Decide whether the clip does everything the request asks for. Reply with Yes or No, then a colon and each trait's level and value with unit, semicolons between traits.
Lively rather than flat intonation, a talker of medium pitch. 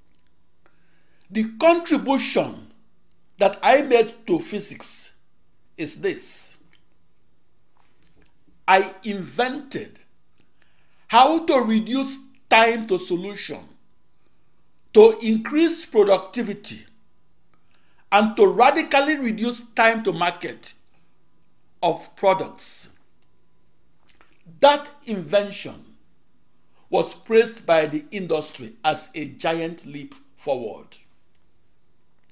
No: wide, 7.3 semitones; high, 205 Hz